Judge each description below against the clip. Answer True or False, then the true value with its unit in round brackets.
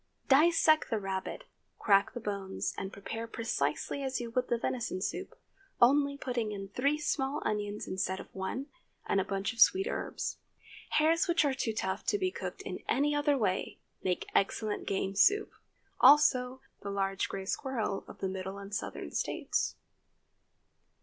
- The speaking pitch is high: True (225 Hz)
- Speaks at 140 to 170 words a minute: True (165 wpm)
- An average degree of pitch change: False (6.2 semitones)